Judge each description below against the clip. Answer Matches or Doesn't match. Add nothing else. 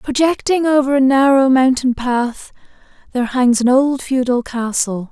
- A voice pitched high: Matches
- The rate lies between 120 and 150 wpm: Matches